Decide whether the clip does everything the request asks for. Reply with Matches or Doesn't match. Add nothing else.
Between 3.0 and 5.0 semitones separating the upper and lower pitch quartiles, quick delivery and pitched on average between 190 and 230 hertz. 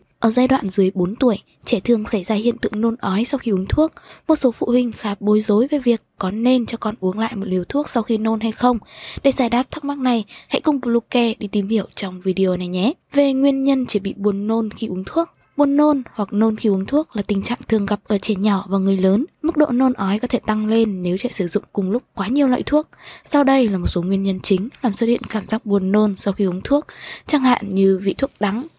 Matches